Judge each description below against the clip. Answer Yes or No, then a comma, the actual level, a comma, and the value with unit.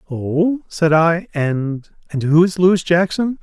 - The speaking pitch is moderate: Yes, medium, 170 Hz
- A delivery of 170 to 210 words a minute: No, average, 140 wpm